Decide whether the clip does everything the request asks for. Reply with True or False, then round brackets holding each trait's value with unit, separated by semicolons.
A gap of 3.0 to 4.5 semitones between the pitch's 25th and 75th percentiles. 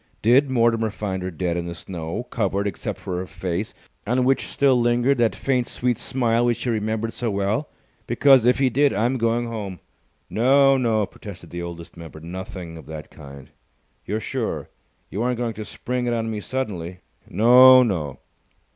False (5.0 semitones)